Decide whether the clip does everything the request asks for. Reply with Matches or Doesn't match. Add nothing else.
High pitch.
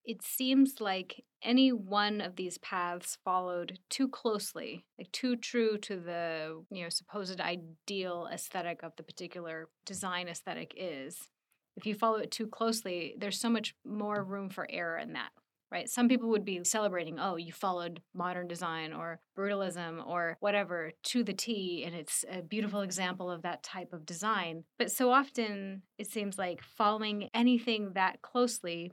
Matches